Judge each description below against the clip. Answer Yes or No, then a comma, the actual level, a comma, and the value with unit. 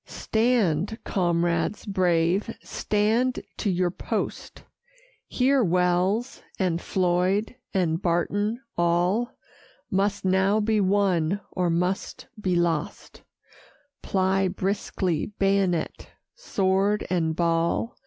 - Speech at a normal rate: No, slow, 95 wpm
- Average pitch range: Yes, average, 3.0 semitones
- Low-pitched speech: No, high, 190 Hz